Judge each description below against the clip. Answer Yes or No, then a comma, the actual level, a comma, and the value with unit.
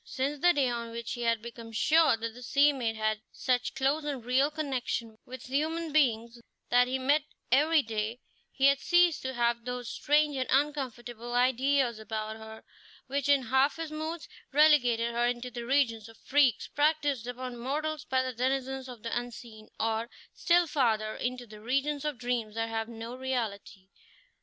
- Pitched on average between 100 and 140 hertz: No, very high, 250 Hz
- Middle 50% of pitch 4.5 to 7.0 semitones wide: No, average, 3.6 semitones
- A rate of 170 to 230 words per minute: Yes, average, 175 wpm